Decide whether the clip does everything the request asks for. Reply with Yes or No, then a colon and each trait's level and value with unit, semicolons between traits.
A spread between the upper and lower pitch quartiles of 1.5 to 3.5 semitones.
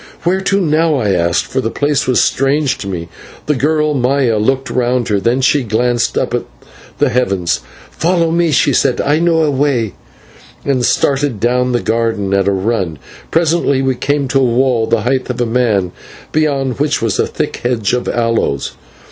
No: average, 4.2 semitones